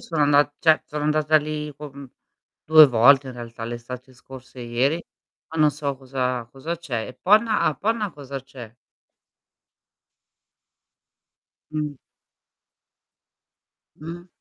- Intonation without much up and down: No, average, 3.2 semitones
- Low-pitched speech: No, medium, 145 Hz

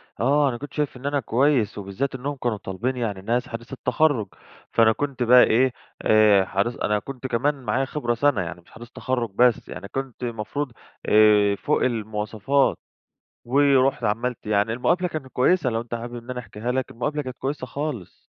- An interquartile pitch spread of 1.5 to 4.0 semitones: Yes, average, 3.7 semitones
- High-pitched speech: No, low, 125 Hz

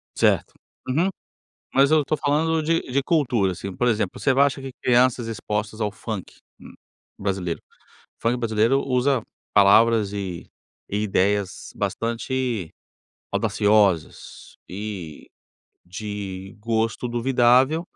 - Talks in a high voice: No, low, 115 Hz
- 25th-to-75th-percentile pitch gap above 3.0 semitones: Yes, average, 4.4 semitones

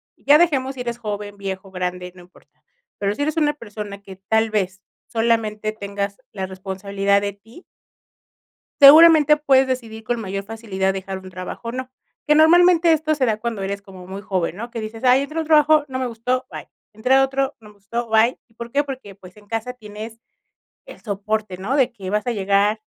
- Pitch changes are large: No, average, 4.6 semitones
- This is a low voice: No, high, 220 Hz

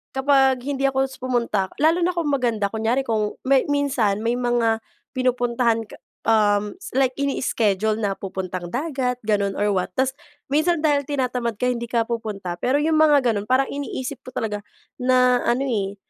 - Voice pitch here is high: Yes, high, 245 Hz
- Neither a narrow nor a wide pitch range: Yes, average, 3.8 semitones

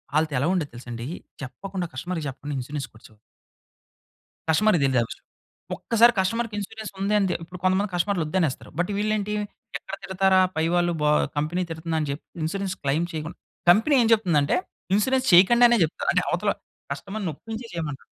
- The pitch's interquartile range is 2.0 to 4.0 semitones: No, average, 5.2 semitones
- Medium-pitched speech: Yes, medium, 180 Hz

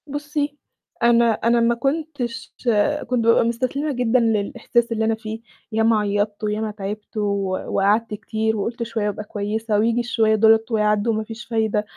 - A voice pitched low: No, high, 225 Hz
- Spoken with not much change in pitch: Yes, narrow, 1.8 semitones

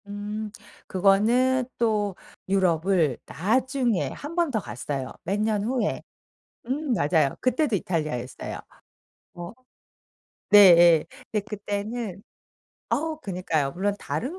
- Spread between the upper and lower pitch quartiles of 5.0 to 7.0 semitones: Yes, wide, 5.5 semitones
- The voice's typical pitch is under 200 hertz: No, high, 205 Hz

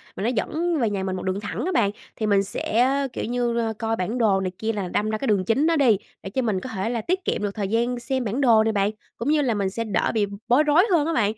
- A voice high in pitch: Yes, high, 225 Hz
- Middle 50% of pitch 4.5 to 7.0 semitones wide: No, average, 4.1 semitones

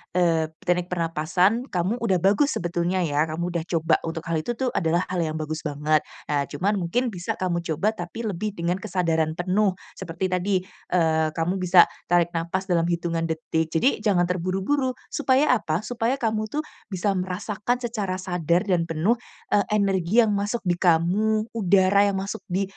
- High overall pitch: No, medium, 180 Hz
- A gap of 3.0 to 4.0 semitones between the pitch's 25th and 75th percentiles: Yes, average, 3.5 semitones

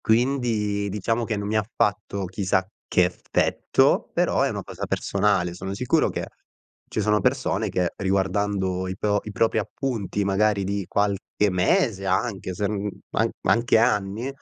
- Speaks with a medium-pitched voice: No, low, 100 Hz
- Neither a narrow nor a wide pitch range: No, narrow, 2.3 semitones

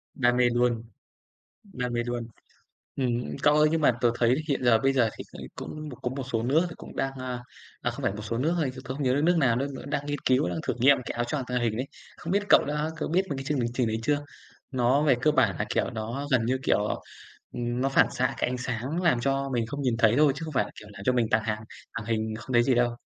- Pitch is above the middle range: No, low, 125 Hz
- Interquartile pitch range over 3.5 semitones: No, average, 3.1 semitones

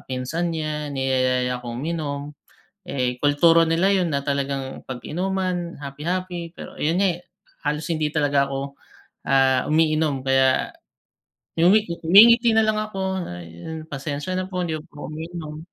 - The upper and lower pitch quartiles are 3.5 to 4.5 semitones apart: Yes, average, 4.1 semitones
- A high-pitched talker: No, medium, 155 Hz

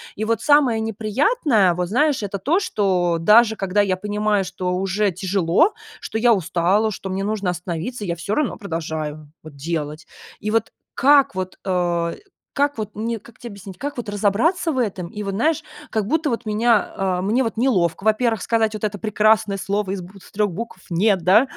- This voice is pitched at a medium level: No, high, 205 Hz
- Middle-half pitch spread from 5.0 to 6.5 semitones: No, average, 3.8 semitones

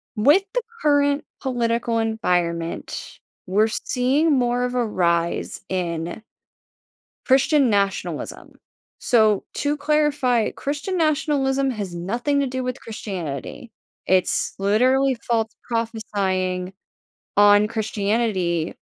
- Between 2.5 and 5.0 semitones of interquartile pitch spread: No, wide, 5.6 semitones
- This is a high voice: Yes, high, 230 Hz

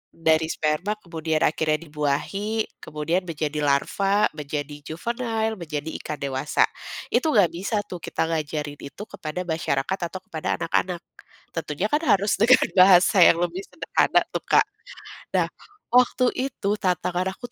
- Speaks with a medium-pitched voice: Yes, medium, 170 Hz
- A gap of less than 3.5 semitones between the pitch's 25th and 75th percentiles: No, average, 4.6 semitones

